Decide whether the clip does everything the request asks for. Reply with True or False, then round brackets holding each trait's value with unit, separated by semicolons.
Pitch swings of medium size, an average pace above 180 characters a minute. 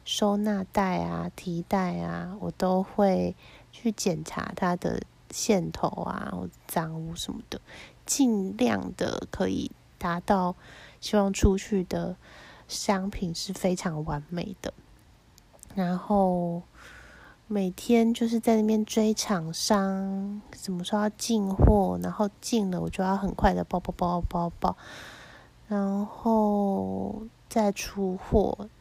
False (3.2 semitones; 170 characters per minute)